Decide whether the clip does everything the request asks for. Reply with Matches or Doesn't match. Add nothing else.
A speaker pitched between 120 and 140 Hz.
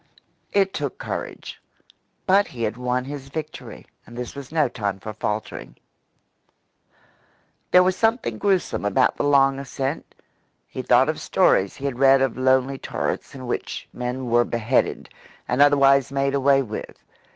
Matches